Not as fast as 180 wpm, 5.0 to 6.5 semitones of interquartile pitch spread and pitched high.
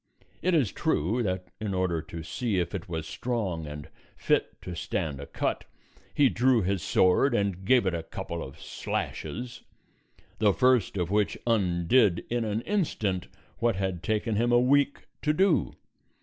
No: average, 165 wpm; wide, 5.5 semitones; low, 100 Hz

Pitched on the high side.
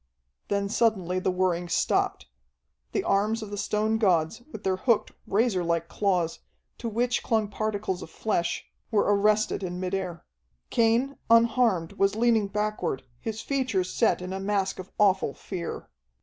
Yes: high, 200 Hz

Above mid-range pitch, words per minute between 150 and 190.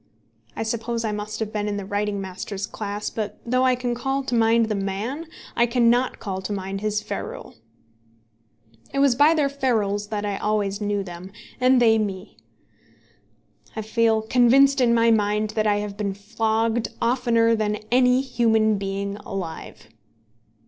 Yes: high, 220 Hz; average, 165 wpm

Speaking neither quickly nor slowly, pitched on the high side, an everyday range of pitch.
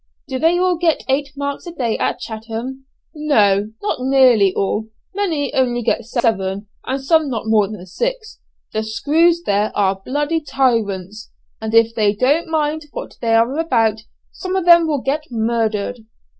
No: average, 160 wpm; high, 245 Hz; wide, 5.8 semitones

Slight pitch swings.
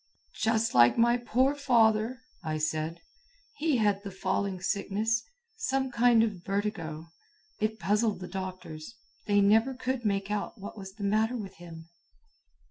No: average, 3.6 semitones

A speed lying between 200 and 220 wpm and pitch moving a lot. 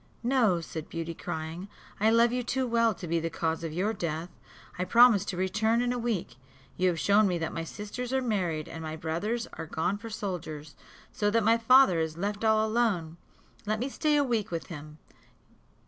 Yes: fast, 205 wpm; wide, 5.7 semitones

